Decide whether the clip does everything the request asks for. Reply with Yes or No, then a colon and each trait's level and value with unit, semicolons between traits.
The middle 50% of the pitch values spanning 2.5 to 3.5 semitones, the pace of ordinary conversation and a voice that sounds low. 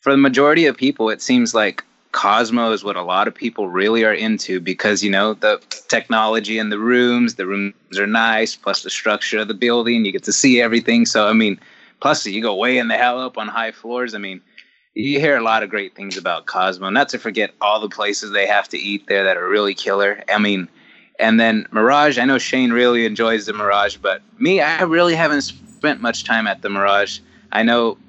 No: average, 2.9 semitones; fast, 225 wpm; low, 115 Hz